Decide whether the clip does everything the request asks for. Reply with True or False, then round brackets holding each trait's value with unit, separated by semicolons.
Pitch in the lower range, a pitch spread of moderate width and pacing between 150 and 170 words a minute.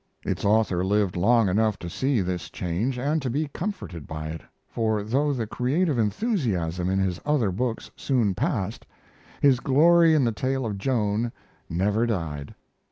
False (110 Hz; 6.0 semitones; 165 wpm)